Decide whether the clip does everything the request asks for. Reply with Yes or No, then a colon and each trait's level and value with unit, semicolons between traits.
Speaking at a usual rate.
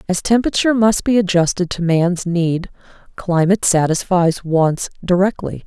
No: slow, 125 wpm